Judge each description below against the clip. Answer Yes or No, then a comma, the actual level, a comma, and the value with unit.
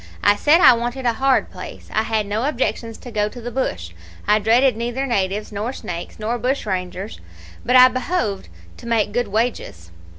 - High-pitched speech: Yes, high, 230 Hz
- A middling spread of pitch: Yes, average, 3.3 semitones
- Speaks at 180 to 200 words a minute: Yes, average, 185 wpm